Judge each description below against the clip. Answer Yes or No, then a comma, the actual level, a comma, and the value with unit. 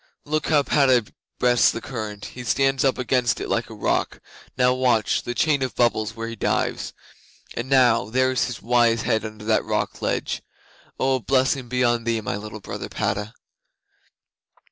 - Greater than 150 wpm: Yes, average, 180 wpm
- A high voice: No, low, 120 Hz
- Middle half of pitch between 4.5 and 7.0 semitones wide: No, narrow, 2.6 semitones